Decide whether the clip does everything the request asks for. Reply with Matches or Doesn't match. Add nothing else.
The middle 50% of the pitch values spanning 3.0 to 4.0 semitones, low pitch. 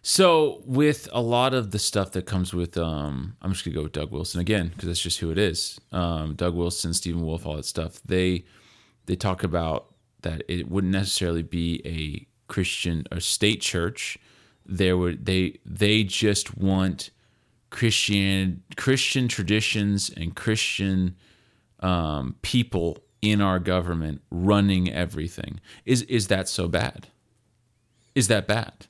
Matches